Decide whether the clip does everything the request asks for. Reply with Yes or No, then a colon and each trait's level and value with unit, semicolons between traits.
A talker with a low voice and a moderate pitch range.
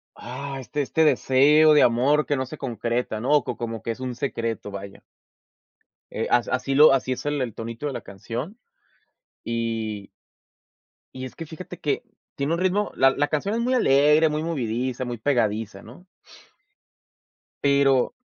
Yes: low, 130 Hz; average, 4.2 semitones